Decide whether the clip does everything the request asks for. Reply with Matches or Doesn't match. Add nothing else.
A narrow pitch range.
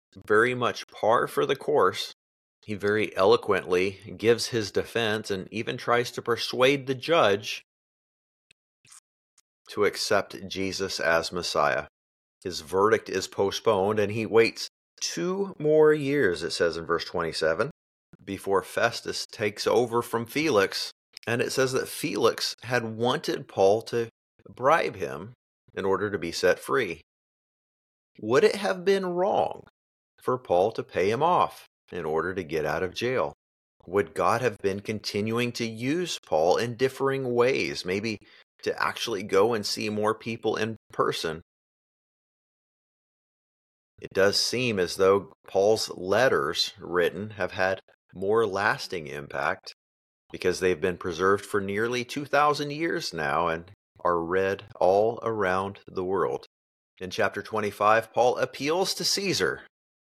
Doesn't match